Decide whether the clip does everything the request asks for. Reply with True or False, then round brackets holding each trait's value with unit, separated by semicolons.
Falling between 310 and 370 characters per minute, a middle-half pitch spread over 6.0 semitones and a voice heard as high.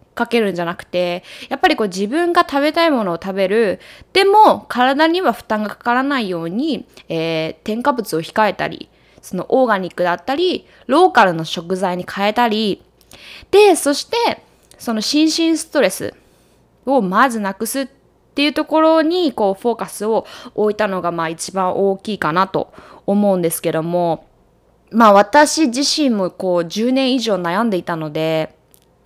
True (315 characters per minute; 7.6 semitones; 215 Hz)